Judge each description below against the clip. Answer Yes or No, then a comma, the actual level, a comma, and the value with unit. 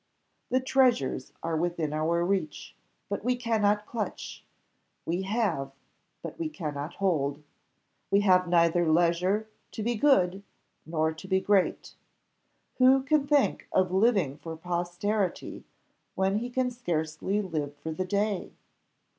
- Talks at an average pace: No, slow, 130 wpm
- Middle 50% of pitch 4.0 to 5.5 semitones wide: Yes, average, 4.8 semitones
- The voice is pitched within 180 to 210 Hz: Yes, medium, 185 Hz